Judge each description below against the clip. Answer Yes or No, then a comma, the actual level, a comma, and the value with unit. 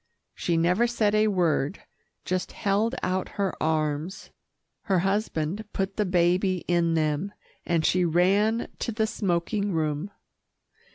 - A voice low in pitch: No, medium, 185 Hz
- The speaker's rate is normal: No, slow, 130 wpm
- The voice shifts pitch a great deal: No, average, 3.5 semitones